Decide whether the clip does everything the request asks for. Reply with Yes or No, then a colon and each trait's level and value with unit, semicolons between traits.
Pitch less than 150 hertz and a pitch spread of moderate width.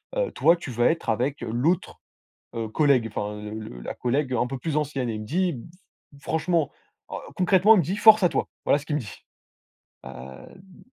No: medium, 140 Hz; wide, 7.0 semitones